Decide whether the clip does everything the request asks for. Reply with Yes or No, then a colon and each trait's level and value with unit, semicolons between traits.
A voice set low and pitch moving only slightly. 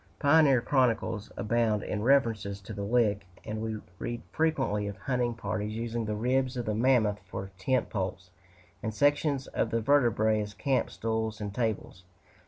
No: low, 115 Hz; average, 3.3 semitones